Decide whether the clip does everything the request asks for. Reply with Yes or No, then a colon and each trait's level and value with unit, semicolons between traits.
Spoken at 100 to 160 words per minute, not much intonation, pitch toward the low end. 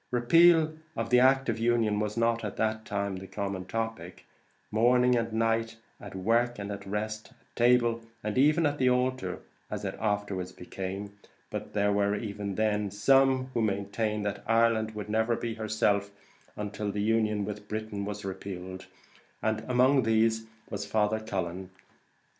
Yes: average, 150 wpm; narrow, 2.3 semitones; low, 110 Hz